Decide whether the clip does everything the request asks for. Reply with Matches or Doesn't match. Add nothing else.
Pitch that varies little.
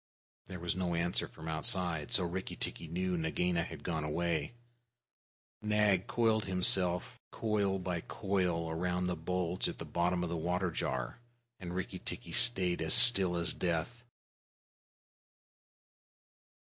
Matches